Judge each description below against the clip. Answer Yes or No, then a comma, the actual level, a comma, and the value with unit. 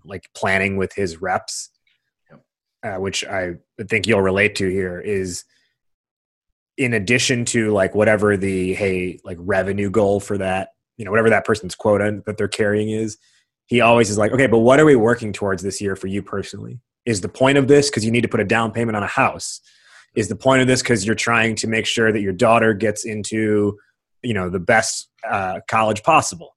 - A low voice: Yes, low, 110 Hz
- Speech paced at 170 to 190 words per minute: No, fast, 205 wpm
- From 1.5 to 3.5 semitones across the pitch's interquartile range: Yes, average, 2.8 semitones